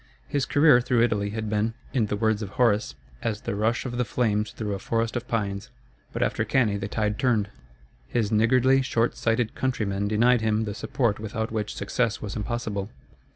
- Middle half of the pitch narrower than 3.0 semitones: Yes, narrow, 2.5 semitones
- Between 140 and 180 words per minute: No, average, 190 wpm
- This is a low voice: Yes, low, 110 Hz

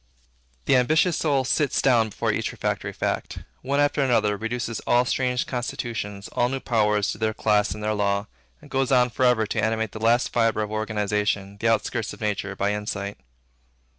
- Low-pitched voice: Yes, low, 110 Hz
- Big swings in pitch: No, average, 3.0 semitones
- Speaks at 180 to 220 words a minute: Yes, average, 185 wpm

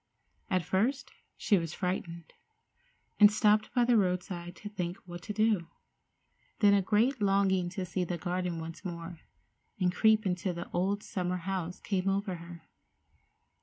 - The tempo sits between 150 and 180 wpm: Yes, average, 155 wpm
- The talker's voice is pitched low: No, medium, 185 Hz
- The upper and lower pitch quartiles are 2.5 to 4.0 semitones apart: Yes, average, 2.8 semitones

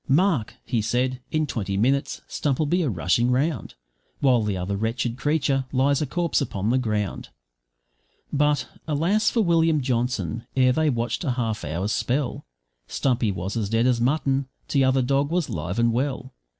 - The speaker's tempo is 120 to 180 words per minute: Yes, average, 165 wpm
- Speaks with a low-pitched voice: Yes, low, 130 Hz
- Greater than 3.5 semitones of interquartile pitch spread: Yes, average, 4.1 semitones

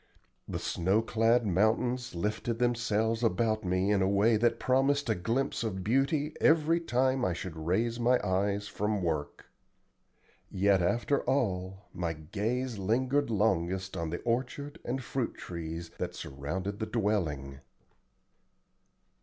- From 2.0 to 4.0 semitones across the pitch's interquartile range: No, average, 4.8 semitones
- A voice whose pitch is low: Yes, low, 110 Hz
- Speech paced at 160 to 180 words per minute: No, slow, 135 wpm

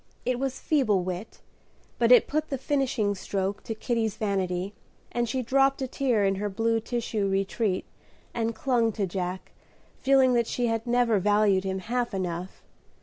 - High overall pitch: Yes, high, 225 Hz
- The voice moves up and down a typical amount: Yes, average, 4.1 semitones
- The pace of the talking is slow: No, average, 165 wpm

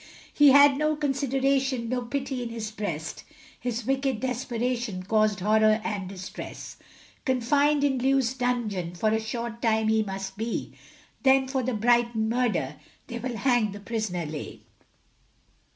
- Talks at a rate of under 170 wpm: Yes, average, 145 wpm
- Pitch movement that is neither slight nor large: Yes, average, 3.5 semitones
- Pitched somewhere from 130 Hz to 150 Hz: No, high, 235 Hz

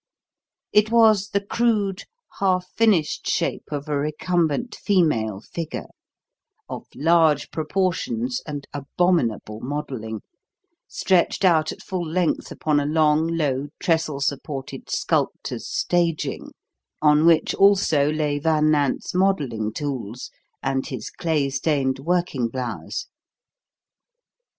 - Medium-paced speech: No, slow, 110 wpm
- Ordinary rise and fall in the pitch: Yes, average, 4.2 semitones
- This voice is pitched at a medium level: Yes, medium, 155 Hz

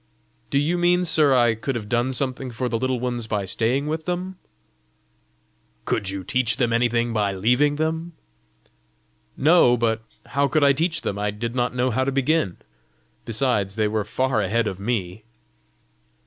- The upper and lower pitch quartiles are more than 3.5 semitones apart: Yes, average, 4.3 semitones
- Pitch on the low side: Yes, low, 125 Hz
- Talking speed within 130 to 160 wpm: No, average, 170 wpm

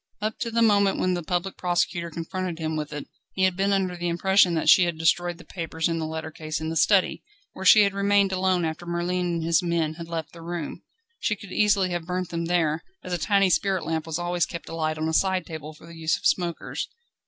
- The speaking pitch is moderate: Yes, medium, 175 Hz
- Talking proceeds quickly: Yes, fast, 245 wpm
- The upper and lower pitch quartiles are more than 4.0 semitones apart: No, narrow, 2.5 semitones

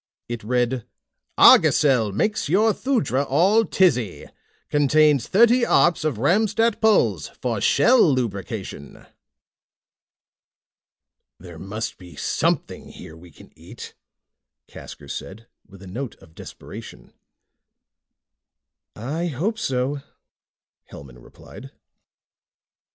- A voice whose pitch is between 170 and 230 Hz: No, low, 130 Hz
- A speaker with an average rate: No, slow, 95 wpm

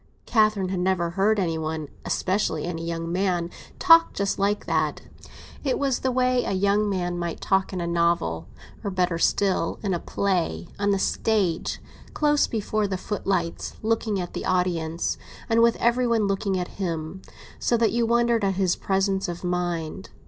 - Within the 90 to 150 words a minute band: No, average, 170 wpm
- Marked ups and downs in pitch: No, average, 3.6 semitones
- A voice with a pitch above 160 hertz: Yes, high, 190 Hz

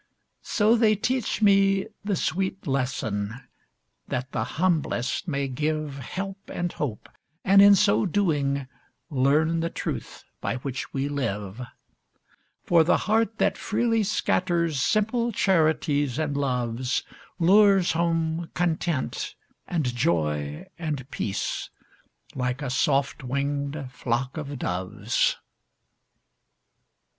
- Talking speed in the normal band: No, slow, 110 wpm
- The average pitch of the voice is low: No, medium, 150 Hz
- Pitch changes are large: Yes, wide, 6.3 semitones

